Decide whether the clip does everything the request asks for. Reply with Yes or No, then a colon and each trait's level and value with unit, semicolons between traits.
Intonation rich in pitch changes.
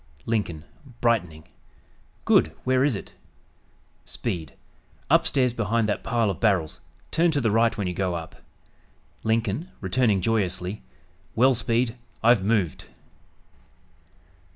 No: average, 4.0 semitones